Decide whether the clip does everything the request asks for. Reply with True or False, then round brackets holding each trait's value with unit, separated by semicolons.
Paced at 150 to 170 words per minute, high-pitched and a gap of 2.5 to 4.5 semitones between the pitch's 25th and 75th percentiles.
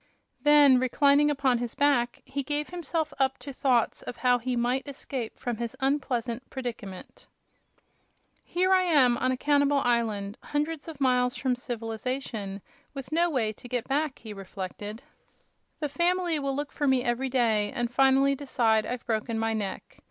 True (165 wpm; 255 Hz; 3.4 semitones)